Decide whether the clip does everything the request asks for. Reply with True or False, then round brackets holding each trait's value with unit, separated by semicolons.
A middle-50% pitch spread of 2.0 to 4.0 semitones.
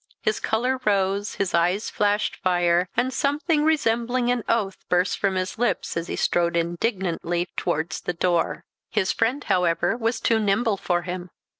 False (4.7 semitones)